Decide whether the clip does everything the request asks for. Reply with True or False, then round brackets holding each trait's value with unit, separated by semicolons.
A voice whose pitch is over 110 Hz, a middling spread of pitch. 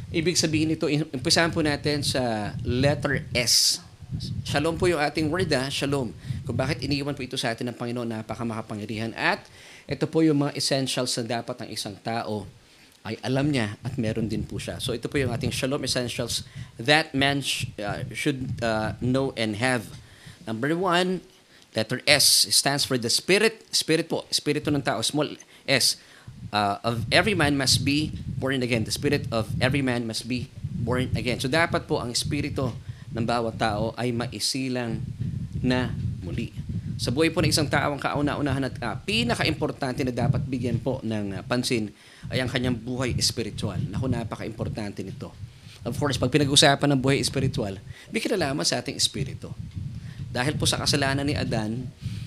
True (130 Hz; 3.5 semitones)